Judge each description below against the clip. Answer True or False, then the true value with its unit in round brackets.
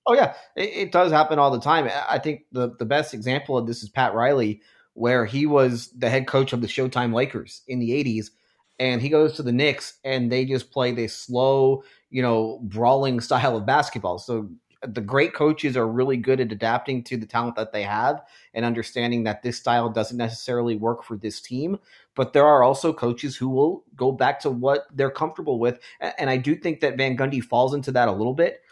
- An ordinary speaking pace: False (215 wpm)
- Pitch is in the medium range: False (125 Hz)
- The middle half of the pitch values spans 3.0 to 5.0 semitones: False (2.6 semitones)